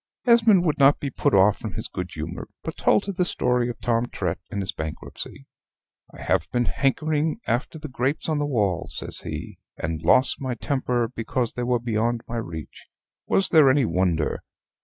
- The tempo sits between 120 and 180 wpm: No, average, 190 wpm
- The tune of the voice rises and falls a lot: Yes, wide, 5.8 semitones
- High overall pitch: No, low, 120 Hz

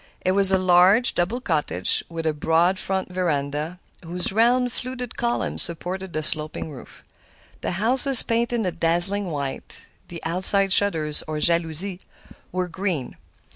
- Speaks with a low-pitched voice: No, medium, 180 Hz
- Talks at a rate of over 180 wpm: No, average, 145 wpm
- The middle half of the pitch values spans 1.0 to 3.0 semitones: No, average, 3.7 semitones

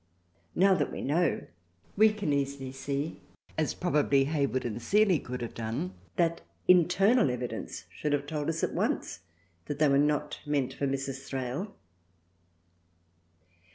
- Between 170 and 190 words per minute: No, average, 145 wpm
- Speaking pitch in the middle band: Yes, medium, 145 Hz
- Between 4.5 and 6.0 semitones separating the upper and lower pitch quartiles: No, average, 3.8 semitones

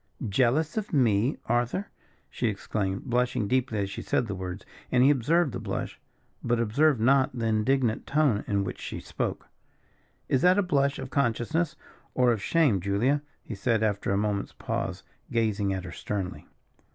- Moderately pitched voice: No, low, 120 Hz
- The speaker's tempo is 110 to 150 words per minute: No, average, 170 wpm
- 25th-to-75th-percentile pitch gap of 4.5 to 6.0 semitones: Yes, average, 5.1 semitones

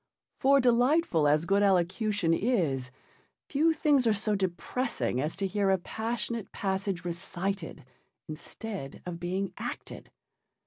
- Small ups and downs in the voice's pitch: No, average, 5.1 semitones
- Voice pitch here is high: Yes, high, 195 Hz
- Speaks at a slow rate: Yes, slow, 125 wpm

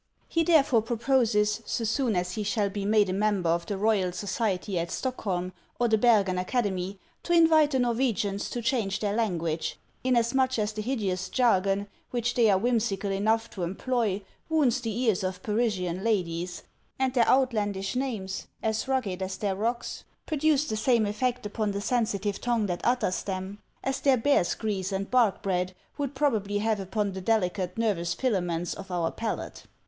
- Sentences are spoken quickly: No, average, 175 wpm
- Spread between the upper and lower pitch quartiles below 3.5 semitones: No, average, 4.1 semitones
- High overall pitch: Yes, high, 210 Hz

